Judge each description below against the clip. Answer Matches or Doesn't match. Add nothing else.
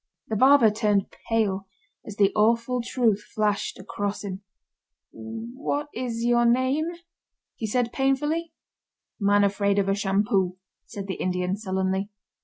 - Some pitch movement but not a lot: Matches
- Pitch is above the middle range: Matches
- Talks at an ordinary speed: Doesn't match